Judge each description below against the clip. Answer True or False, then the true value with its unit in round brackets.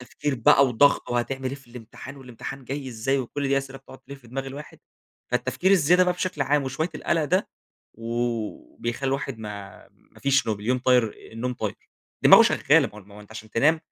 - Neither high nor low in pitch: False (130 Hz)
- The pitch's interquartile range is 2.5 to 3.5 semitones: True (3.2 semitones)